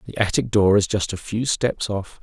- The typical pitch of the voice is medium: No, low, 100 Hz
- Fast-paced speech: Yes, fast, 245 wpm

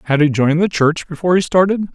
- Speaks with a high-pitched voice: No, medium, 165 Hz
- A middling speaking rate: No, fast, 245 wpm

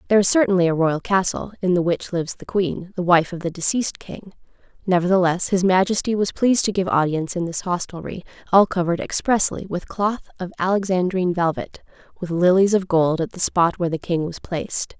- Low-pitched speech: No, medium, 180 Hz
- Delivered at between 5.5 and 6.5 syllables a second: Yes, 5.9 syllables/s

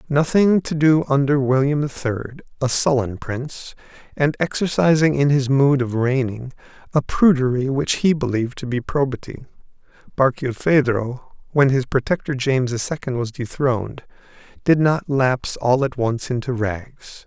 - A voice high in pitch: No, low, 135 Hz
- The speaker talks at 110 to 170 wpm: Yes, average, 145 wpm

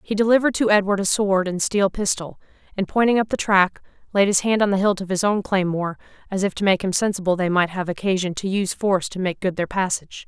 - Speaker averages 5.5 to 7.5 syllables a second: Yes, 6.3 syllables/s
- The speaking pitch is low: No, high, 195 Hz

